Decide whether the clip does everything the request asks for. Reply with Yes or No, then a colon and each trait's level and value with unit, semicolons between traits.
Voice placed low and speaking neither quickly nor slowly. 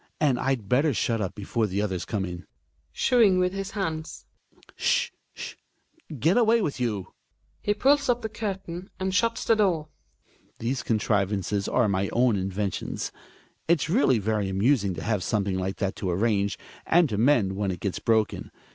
Yes: low, 115 Hz; average, 170 wpm